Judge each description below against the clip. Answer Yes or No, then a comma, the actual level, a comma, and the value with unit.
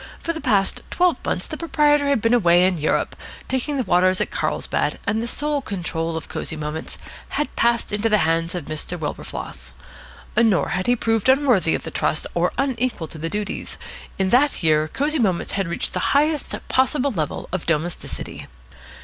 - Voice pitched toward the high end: Yes, high, 205 Hz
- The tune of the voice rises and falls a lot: Yes, wide, 7.6 semitones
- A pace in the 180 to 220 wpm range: Yes, average, 185 wpm